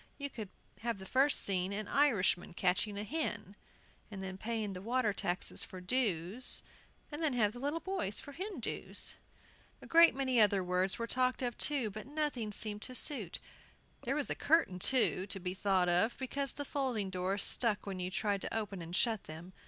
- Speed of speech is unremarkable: Yes, average, 190 wpm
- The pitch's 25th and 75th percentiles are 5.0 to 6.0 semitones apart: Yes, wide, 5.5 semitones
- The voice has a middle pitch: No, high, 215 Hz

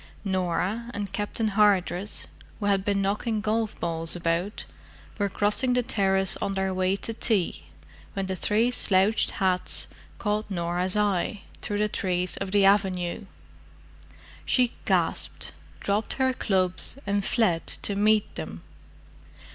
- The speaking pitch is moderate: No, high, 200 Hz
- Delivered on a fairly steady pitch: Yes, narrow, 2.2 semitones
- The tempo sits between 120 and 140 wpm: Yes, slow, 135 wpm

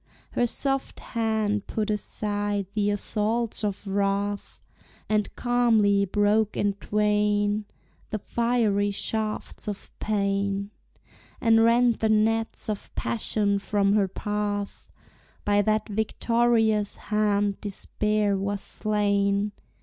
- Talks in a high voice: Yes, high, 210 Hz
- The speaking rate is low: Yes, slow, 105 wpm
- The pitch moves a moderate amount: No, narrow, 1.4 semitones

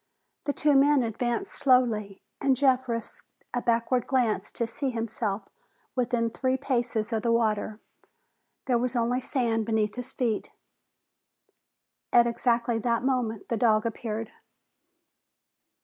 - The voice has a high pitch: Yes, high, 235 Hz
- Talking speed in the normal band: No, slow, 130 wpm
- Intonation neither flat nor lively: No, narrow, 2.1 semitones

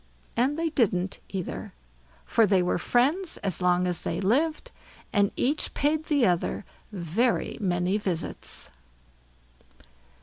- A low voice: No, high, 205 Hz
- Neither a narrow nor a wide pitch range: No, wide, 7.9 semitones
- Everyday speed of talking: No, slow, 125 wpm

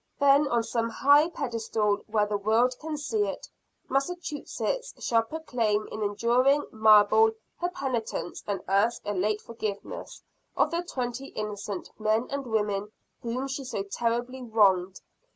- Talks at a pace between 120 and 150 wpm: Yes, average, 140 wpm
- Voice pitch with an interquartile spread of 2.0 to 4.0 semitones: No, average, 4.5 semitones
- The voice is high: Yes, high, 230 Hz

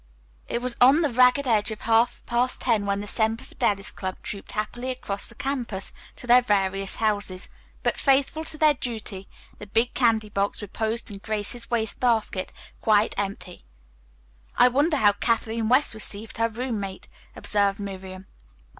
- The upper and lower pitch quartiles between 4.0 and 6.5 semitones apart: No, average, 3.4 semitones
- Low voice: No, high, 220 Hz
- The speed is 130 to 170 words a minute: Yes, average, 160 wpm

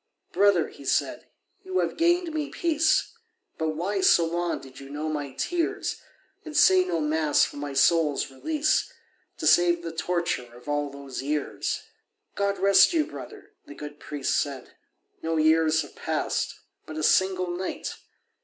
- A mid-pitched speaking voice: Yes, medium, 165 Hz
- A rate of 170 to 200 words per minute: No, average, 155 wpm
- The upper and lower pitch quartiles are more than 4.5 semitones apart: Yes, average, 5.3 semitones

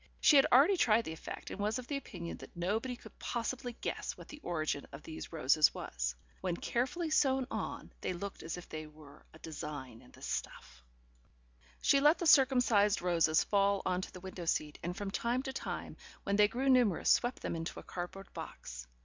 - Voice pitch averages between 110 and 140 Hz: No, high, 195 Hz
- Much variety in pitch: Yes, wide, 7.5 semitones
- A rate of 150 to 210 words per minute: Yes, average, 200 wpm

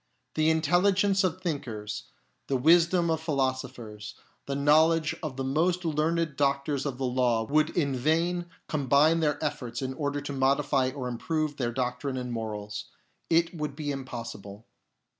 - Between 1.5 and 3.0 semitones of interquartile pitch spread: No, average, 3.9 semitones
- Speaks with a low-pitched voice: No, medium, 145 Hz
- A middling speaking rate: Yes, average, 155 wpm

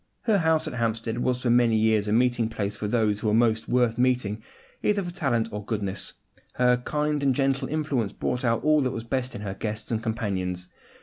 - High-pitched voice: No, low, 115 Hz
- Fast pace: Yes, fast, 210 wpm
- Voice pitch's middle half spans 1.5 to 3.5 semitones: Yes, average, 3.1 semitones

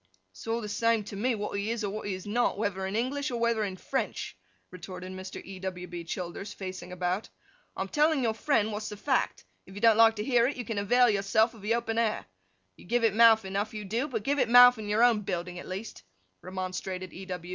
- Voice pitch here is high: Yes, high, 210 Hz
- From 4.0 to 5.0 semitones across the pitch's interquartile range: No, average, 3.5 semitones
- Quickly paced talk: Yes, fast, 245 wpm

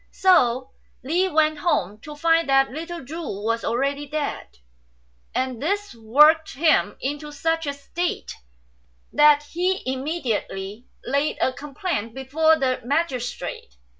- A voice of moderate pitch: No, very high, 285 Hz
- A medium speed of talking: No, slow, 125 wpm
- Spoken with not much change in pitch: No, average, 4.0 semitones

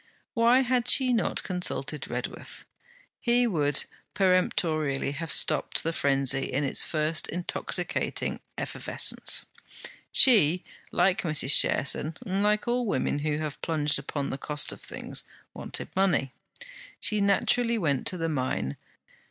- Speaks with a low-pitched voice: No, medium, 165 Hz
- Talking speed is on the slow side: Yes, slow, 125 wpm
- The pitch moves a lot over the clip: Yes, wide, 6.3 semitones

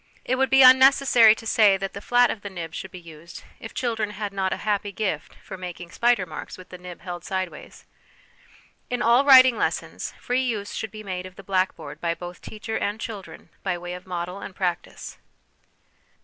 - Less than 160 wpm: No, fast, 205 wpm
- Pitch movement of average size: Yes, average, 4.0 semitones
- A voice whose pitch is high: Yes, high, 200 Hz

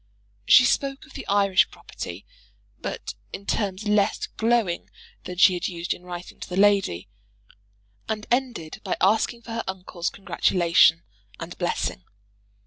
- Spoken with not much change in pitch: No, average, 3.9 semitones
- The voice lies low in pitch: No, high, 195 Hz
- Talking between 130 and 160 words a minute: Yes, average, 140 wpm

